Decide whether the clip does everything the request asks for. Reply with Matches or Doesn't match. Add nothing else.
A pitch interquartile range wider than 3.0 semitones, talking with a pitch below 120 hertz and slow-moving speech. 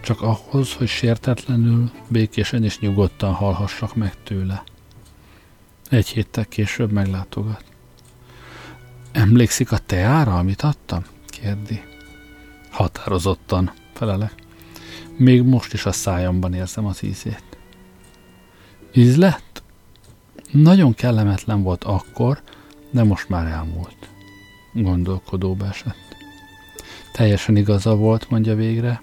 Matches